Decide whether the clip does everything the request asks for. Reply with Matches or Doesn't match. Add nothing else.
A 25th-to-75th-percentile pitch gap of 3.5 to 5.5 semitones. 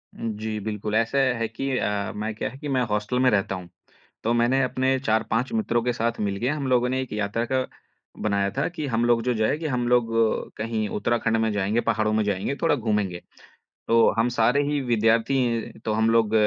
Doesn't match